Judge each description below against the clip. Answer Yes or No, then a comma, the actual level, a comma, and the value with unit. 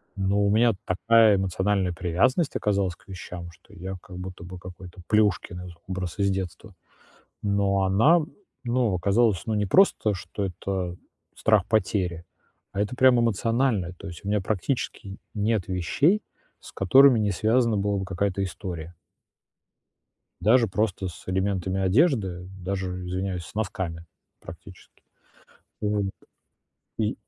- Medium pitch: No, very low, 95 Hz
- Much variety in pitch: No, average, 2.9 semitones